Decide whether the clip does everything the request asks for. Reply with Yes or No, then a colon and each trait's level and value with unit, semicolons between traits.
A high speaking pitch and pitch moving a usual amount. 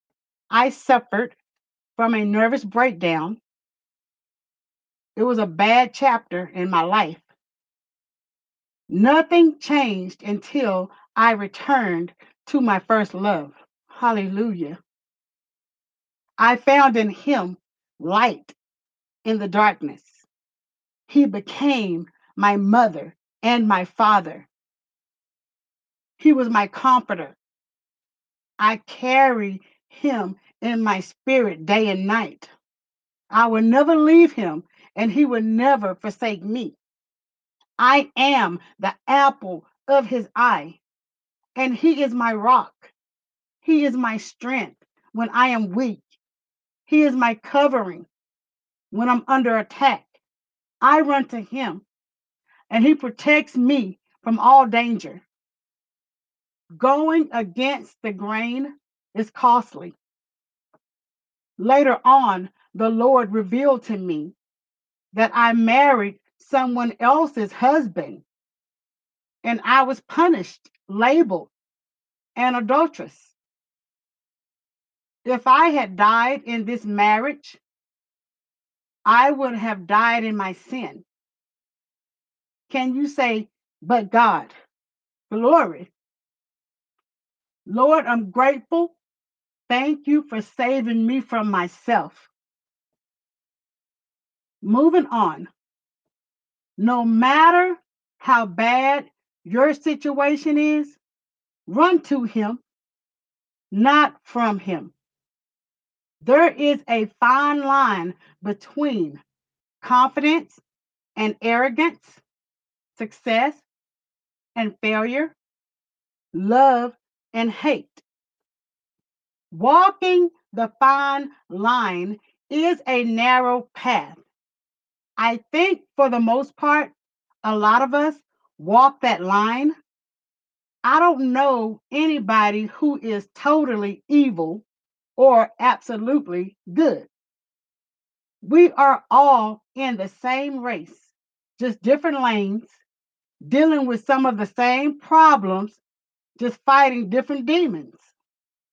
Yes: high, 245 Hz; average, 4.6 semitones